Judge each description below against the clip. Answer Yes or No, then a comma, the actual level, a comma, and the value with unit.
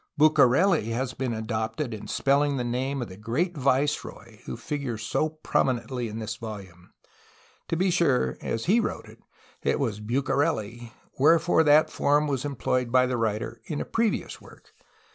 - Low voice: Yes, low, 130 Hz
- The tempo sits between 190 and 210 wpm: No, average, 160 wpm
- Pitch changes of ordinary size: Yes, average, 4.4 semitones